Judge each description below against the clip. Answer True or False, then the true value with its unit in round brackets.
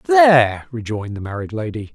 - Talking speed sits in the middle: True (155 wpm)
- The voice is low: True (130 Hz)